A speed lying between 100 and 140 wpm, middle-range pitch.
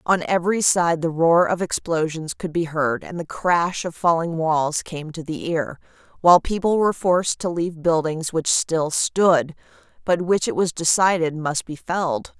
No: average, 185 wpm; medium, 165 Hz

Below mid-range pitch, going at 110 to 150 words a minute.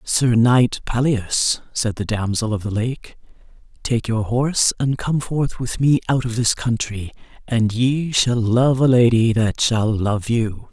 No: low, 120 Hz; average, 175 wpm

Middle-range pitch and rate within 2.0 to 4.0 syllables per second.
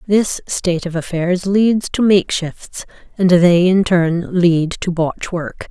Yes: medium, 180 Hz; 3.7 syllables/s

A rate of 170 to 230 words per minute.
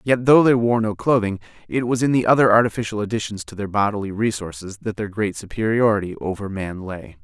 Yes: average, 200 wpm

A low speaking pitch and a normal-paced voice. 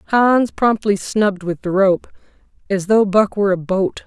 No: high, 200 Hz; average, 175 wpm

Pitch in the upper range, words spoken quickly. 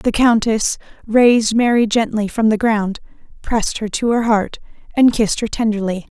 No: high, 220 Hz; average, 165 wpm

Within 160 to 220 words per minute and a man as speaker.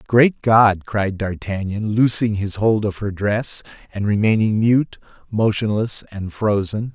No: average, 140 wpm; male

